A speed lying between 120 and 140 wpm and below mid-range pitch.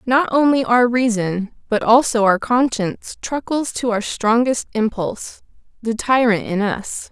No: slow, 135 wpm; high, 230 Hz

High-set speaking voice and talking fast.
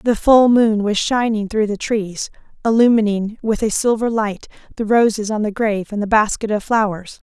No: high, 215 Hz; average, 190 wpm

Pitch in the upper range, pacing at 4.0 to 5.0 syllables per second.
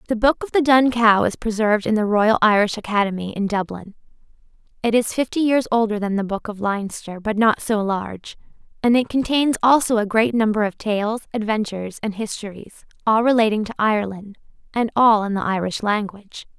No: high, 215 Hz; 5.5 syllables/s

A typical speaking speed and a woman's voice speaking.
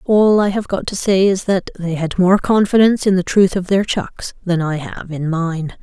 No: fast, 235 wpm; female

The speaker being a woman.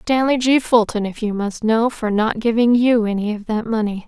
Yes: female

